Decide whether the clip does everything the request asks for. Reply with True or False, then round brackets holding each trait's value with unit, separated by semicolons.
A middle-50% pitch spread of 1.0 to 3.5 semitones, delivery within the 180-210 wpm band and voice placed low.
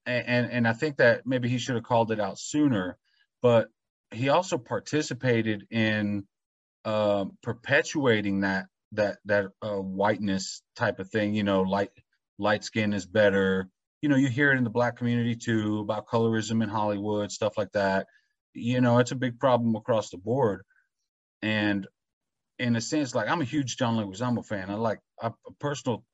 True (3.1 semitones; 185 wpm; 115 Hz)